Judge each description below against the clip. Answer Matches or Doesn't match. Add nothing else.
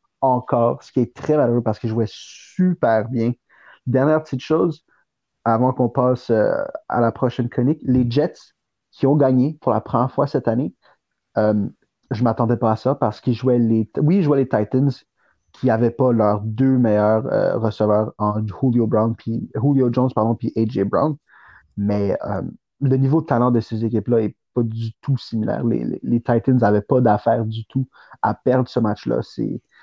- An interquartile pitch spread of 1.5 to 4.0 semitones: Matches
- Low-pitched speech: Matches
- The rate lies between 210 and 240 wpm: Doesn't match